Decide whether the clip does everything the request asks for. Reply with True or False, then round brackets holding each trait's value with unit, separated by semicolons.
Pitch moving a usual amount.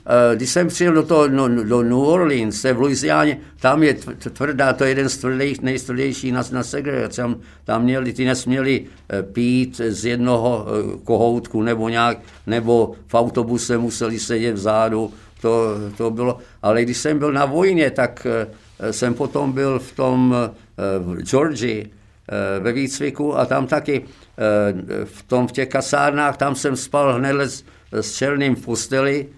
True (3.0 semitones)